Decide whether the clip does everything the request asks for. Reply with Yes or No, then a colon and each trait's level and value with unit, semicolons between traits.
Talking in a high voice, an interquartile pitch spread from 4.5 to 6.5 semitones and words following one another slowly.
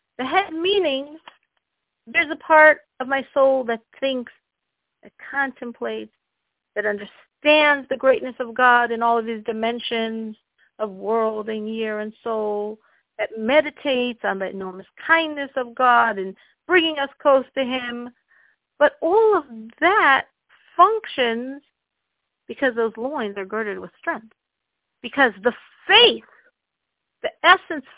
Yes: very high, 255 Hz; average, 4.8 semitones; slow, 130 wpm